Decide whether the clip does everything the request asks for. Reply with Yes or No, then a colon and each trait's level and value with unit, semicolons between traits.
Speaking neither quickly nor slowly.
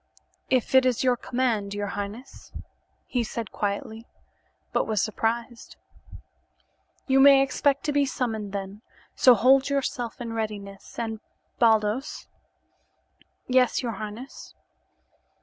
No: slow, 125 wpm